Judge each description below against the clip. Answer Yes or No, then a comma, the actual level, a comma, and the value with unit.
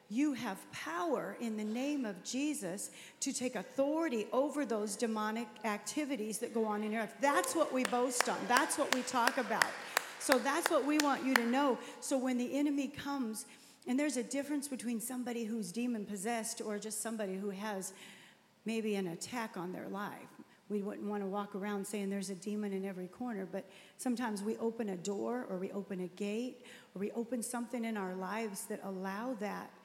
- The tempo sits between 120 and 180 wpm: No, average, 195 wpm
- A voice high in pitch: Yes, high, 225 Hz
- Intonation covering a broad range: No, average, 3.7 semitones